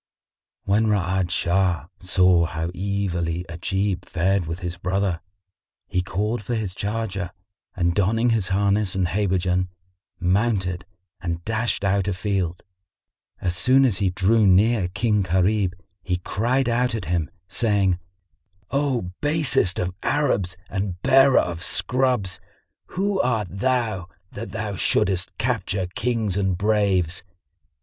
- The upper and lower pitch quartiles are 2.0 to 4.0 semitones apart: Yes, average, 3.5 semitones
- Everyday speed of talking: No, slow, 130 wpm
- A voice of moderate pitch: No, very low, 95 Hz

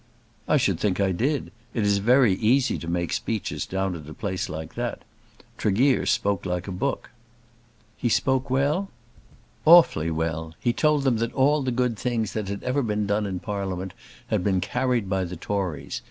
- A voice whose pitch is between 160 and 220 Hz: No, low, 105 Hz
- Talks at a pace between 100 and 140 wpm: No, average, 185 wpm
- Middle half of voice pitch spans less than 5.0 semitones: No, wide, 5.4 semitones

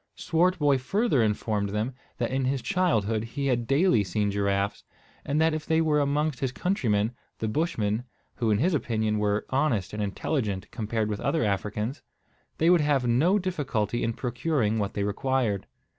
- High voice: No, low, 120 Hz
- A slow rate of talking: No, average, 170 wpm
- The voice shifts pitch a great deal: Yes, wide, 6.1 semitones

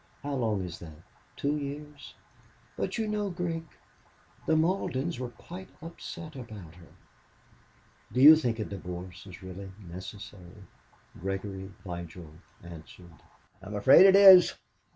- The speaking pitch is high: No, low, 110 Hz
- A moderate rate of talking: No, slow, 130 wpm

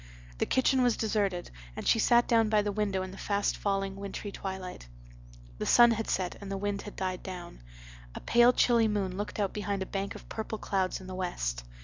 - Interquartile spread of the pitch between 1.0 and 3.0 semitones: Yes, narrow, 2.4 semitones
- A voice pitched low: No, high, 200 Hz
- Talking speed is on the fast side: Yes, fast, 215 wpm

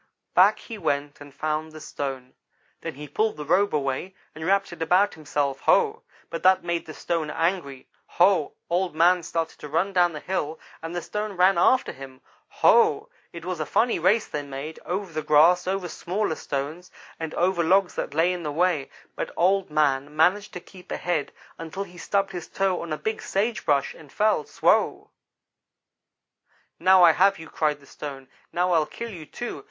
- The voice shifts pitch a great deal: No, average, 3.9 semitones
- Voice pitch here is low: No, medium, 170 Hz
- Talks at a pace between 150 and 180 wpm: No, average, 190 wpm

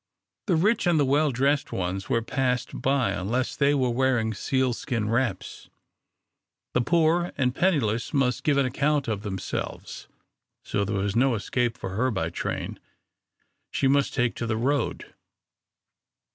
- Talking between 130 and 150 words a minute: Yes, average, 145 wpm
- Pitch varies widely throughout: No, average, 4.1 semitones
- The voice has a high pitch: No, low, 125 Hz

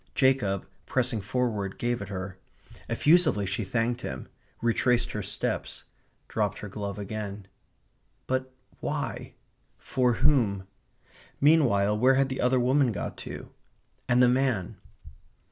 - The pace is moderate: No, slow, 125 wpm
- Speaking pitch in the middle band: No, low, 120 Hz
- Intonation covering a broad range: No, average, 4.4 semitones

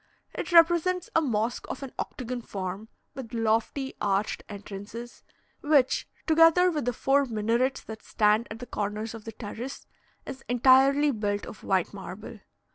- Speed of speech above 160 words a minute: No, average, 150 wpm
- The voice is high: Yes, high, 240 Hz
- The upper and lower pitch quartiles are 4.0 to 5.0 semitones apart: Yes, average, 4.4 semitones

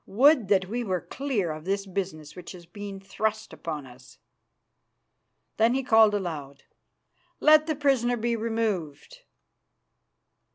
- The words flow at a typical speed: No, slow, 130 wpm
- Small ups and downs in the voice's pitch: No, average, 5.3 semitones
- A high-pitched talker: Yes, high, 205 Hz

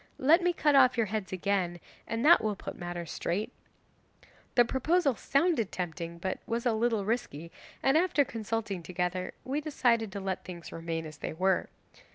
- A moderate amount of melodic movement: No, wide, 6.5 semitones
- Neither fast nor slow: Yes, average, 175 wpm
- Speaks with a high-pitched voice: Yes, high, 215 Hz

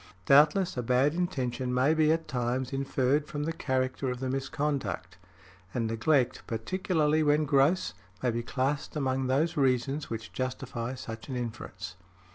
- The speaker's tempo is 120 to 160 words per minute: Yes, average, 150 wpm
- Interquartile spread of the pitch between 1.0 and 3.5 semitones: Yes, average, 3.1 semitones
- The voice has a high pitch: No, low, 135 Hz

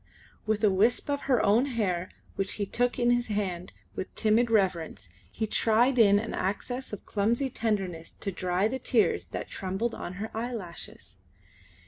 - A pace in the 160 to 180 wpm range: Yes, average, 165 wpm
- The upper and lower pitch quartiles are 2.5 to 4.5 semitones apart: Yes, average, 3.9 semitones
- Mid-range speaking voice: No, high, 215 Hz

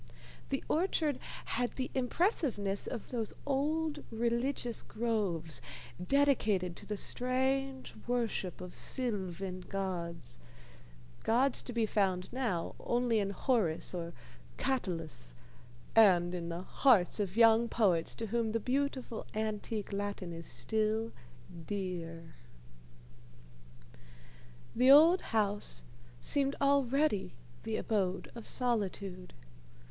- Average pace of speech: No, slow, 105 wpm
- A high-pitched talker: Yes, high, 220 Hz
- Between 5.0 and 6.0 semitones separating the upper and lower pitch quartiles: Yes, wide, 5.6 semitones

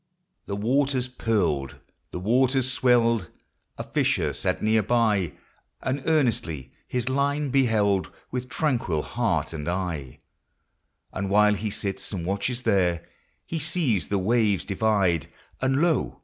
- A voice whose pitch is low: Yes, low, 110 Hz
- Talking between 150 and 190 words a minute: No, slow, 135 wpm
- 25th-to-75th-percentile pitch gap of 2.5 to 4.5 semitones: No, average, 5.3 semitones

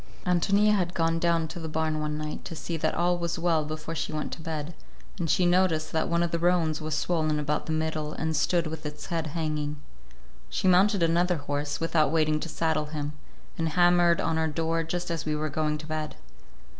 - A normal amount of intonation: No, narrow, 1.9 semitones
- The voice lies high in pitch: No, medium, 160 Hz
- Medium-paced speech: No, fast, 215 wpm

